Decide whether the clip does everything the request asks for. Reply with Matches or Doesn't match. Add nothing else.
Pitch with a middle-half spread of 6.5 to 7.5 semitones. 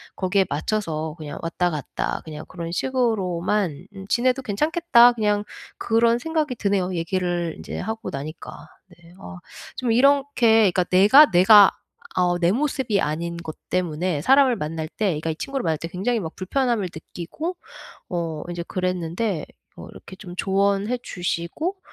Doesn't match